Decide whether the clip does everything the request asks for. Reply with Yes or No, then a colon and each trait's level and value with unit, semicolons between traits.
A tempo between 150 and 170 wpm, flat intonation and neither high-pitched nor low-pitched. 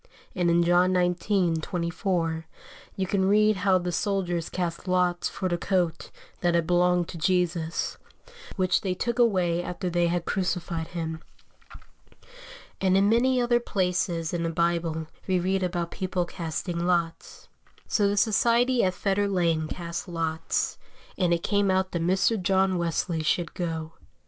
Yes: average, 155 wpm; narrow, 2.1 semitones; medium, 180 Hz